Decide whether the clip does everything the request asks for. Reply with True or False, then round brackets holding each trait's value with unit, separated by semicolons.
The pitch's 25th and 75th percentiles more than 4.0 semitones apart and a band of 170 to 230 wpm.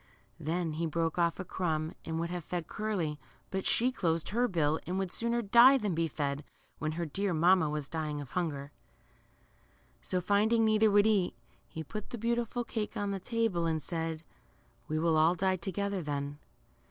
True (4.5 semitones; 190 wpm)